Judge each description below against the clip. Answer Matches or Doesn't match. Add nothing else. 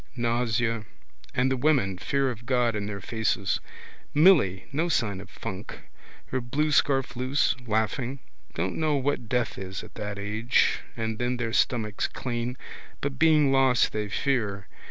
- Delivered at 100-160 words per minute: Matches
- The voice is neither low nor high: Doesn't match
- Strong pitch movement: Doesn't match